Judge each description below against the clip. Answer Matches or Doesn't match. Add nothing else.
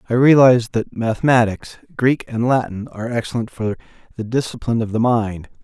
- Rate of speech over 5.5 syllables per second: Matches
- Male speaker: Matches